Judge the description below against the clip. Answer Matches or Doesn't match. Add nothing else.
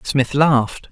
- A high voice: Doesn't match